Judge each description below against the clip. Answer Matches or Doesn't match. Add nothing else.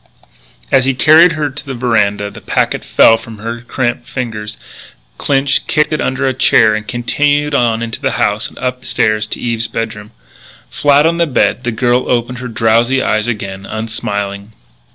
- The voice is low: Matches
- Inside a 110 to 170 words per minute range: Doesn't match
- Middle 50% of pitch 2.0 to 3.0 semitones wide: Doesn't match